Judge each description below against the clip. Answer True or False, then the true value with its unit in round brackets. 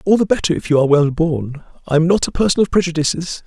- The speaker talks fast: True (240 wpm)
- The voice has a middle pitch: True (165 Hz)